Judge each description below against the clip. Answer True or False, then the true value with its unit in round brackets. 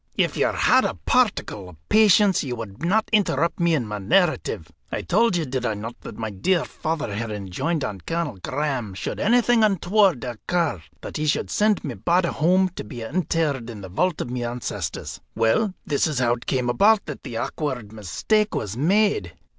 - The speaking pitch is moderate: True (145 Hz)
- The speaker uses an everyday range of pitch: False (8.6 semitones)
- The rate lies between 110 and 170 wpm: False (195 wpm)